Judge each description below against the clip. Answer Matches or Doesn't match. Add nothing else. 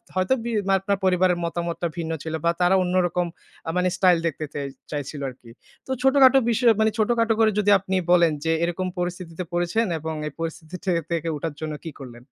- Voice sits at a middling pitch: Matches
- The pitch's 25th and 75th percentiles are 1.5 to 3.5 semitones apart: Matches